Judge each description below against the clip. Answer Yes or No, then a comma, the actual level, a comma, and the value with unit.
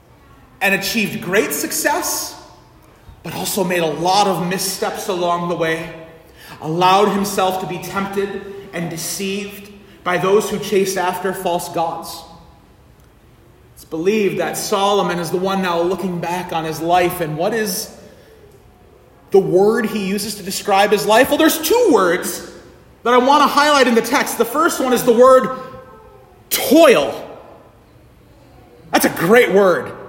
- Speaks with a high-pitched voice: Yes, high, 195 Hz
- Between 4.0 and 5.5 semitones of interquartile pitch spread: No, average, 3.6 semitones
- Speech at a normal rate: Yes, average, 150 wpm